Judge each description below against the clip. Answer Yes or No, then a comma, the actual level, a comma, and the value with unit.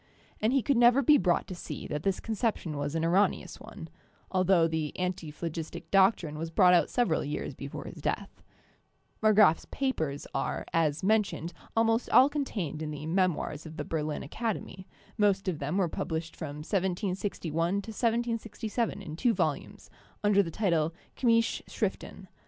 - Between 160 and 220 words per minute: Yes, average, 165 wpm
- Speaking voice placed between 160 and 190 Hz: Yes, medium, 185 Hz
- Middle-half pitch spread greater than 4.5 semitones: Yes, wide, 5.4 semitones